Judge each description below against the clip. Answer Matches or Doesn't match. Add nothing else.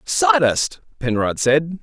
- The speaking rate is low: Matches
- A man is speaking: Matches